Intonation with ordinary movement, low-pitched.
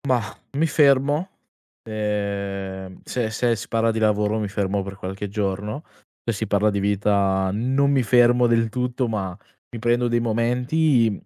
Yes: average, 3.4 semitones; low, 110 Hz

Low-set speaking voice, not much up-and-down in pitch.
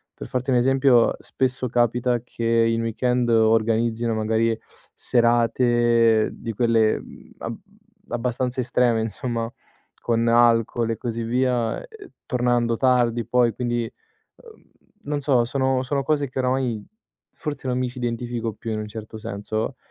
Yes: low, 120 Hz; narrow, 1.7 semitones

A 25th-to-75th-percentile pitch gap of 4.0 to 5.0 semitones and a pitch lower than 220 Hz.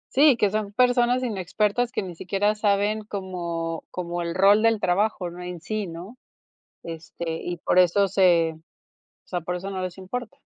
No: average, 3.5 semitones; high, 190 Hz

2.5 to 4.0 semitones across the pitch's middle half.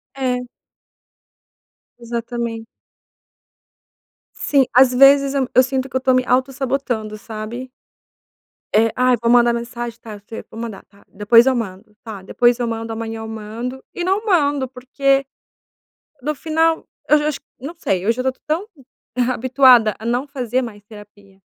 Yes: average, 3.0 semitones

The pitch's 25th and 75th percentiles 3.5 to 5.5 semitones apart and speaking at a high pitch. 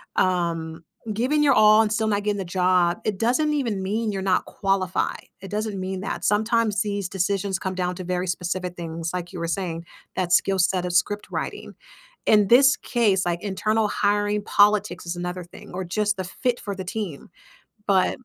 No: average, 2.8 semitones; high, 195 Hz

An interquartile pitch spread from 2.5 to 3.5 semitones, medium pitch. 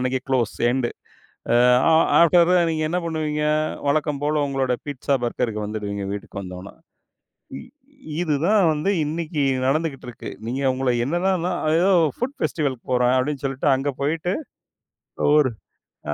No: average, 4.3 semitones; medium, 145 Hz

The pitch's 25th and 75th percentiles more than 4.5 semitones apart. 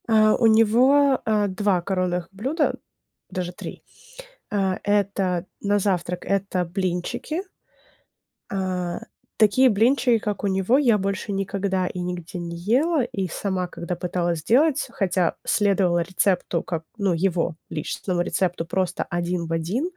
No: average, 3.1 semitones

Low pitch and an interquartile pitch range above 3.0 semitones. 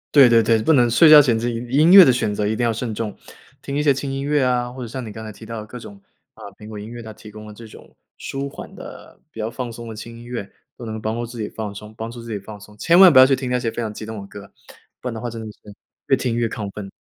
No: low, 115 Hz; average, 2.7 semitones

